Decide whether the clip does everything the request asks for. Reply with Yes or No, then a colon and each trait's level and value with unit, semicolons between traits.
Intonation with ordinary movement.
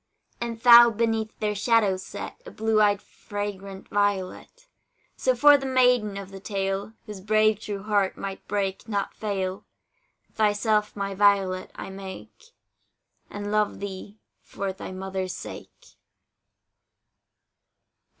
No: narrow, 2.1 semitones